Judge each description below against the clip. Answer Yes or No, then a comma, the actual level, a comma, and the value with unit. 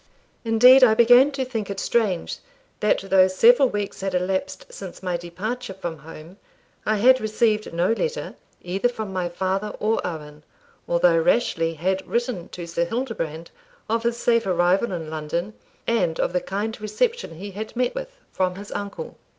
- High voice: Yes, high, 200 Hz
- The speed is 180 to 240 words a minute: No, average, 165 wpm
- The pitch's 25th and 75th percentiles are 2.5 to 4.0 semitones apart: No, average, 4.9 semitones